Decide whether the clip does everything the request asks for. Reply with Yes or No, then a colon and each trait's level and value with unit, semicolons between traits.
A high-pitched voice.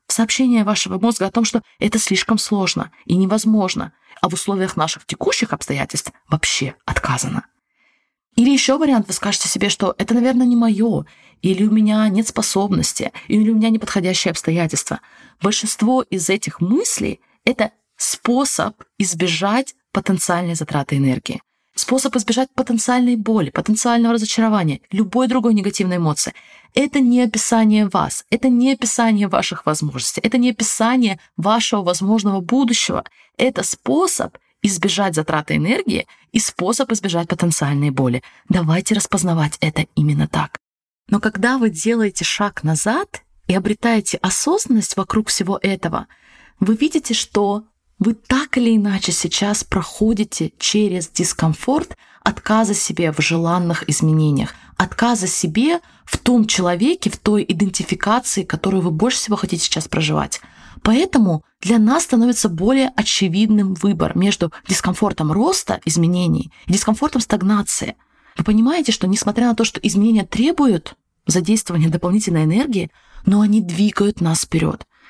Yes: high, 205 Hz